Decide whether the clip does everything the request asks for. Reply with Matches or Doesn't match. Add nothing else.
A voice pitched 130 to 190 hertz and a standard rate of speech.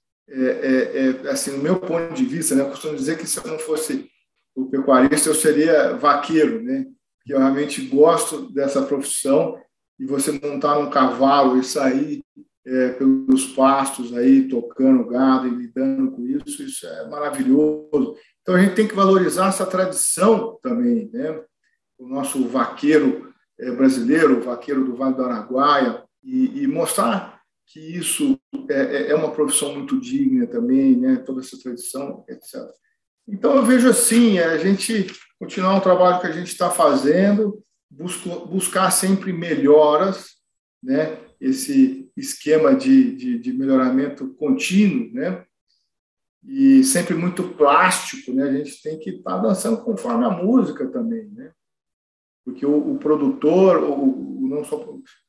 Matches